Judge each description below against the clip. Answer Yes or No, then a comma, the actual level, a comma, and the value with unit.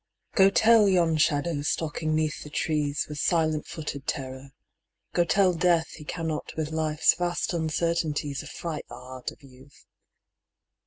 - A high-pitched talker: No, medium, 155 Hz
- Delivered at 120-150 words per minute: Yes, average, 145 wpm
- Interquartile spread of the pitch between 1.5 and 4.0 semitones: Yes, narrow, 2.5 semitones